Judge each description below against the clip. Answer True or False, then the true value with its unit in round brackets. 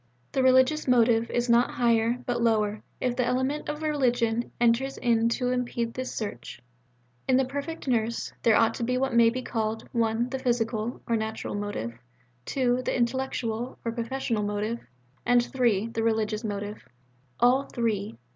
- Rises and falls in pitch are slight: True (2.1 semitones)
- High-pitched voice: True (235 Hz)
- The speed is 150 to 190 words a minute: True (165 wpm)